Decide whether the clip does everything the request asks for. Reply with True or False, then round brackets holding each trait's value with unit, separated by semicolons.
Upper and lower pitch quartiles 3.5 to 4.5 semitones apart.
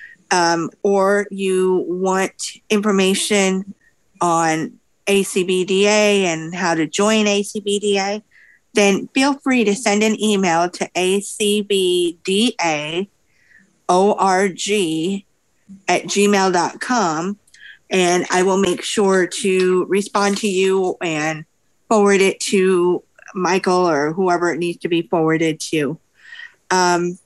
False (2.4 semitones)